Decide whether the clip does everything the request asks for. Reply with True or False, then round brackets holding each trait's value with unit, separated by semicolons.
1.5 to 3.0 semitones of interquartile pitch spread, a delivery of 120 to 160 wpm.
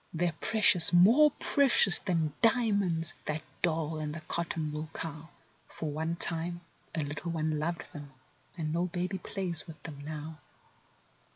True (2.4 semitones; 150 wpm)